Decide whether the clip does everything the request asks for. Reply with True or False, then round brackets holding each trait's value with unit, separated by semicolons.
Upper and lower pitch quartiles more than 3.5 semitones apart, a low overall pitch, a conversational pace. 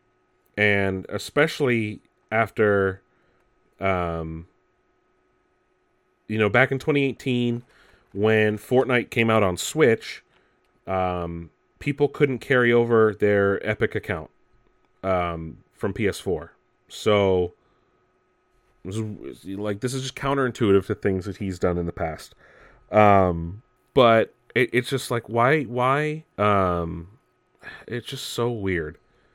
False (4.5 semitones; 105 Hz; 110 wpm)